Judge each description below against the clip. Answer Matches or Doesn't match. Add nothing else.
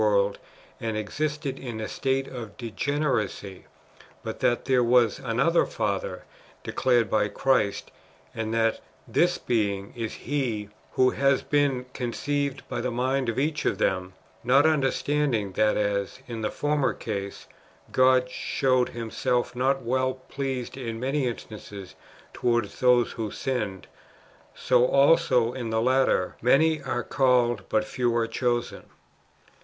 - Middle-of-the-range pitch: Doesn't match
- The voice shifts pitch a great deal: Doesn't match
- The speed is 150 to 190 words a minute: Doesn't match